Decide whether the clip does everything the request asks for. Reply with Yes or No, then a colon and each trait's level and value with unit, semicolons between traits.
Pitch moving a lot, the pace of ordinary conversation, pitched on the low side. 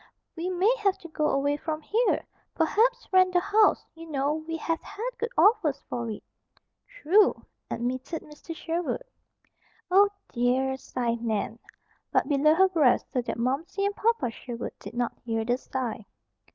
No: wide, 7.2 semitones; average, 160 wpm; very high, 315 Hz